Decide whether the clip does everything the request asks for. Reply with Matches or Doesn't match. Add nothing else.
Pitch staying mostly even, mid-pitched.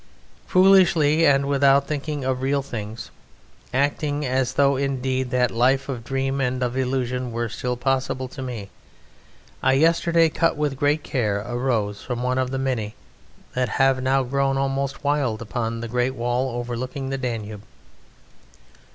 Doesn't match